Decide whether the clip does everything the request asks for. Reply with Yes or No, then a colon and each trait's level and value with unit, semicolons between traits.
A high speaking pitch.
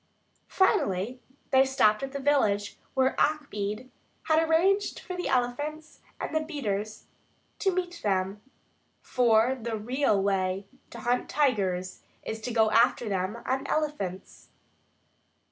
Yes: high, 245 Hz